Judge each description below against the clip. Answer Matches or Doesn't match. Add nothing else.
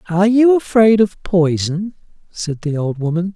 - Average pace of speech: Matches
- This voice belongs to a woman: Doesn't match